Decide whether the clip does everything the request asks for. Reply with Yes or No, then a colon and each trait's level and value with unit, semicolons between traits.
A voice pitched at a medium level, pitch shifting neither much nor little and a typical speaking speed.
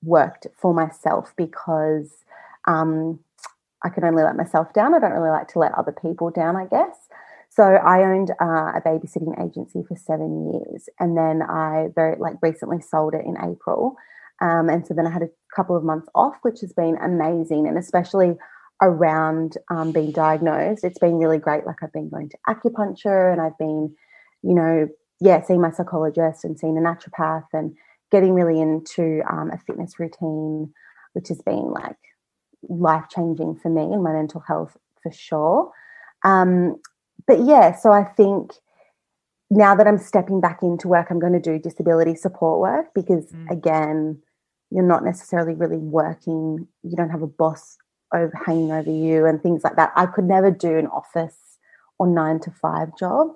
No: medium, 165 Hz; narrow, 2.1 semitones; average, 180 wpm